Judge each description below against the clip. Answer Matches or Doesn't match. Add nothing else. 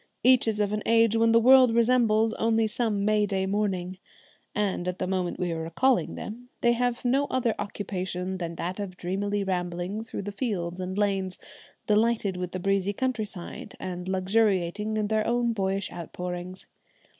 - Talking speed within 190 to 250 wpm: Doesn't match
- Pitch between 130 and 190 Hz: Doesn't match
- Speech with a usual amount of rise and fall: Matches